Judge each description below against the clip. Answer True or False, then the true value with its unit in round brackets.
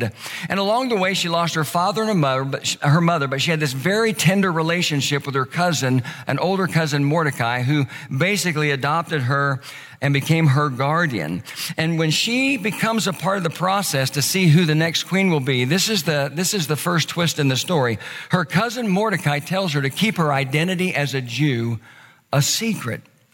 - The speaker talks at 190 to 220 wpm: True (205 wpm)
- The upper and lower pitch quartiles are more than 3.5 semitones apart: True (4.6 semitones)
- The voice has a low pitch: False (160 Hz)